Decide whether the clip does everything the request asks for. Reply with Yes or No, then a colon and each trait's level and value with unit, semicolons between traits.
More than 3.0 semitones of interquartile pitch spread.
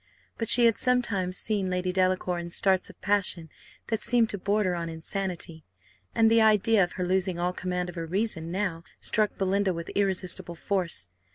No: average, 2.7 semitones